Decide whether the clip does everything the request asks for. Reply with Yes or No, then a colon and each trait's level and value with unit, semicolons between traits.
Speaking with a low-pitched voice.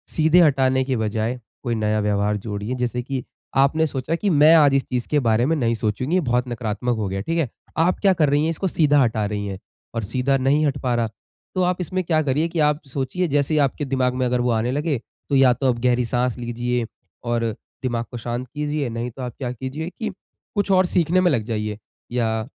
Yes: low, 130 Hz